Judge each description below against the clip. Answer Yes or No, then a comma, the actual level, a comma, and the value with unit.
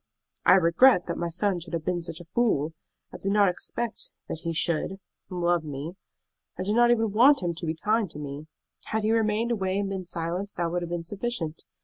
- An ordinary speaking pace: No, fast, 220 wpm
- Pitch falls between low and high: Yes, medium, 180 Hz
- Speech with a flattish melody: No, average, 4.1 semitones